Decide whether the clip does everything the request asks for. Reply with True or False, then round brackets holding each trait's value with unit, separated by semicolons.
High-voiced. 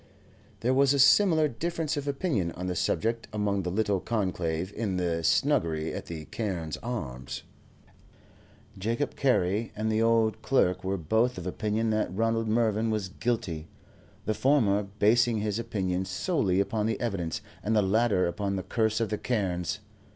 False (105 Hz)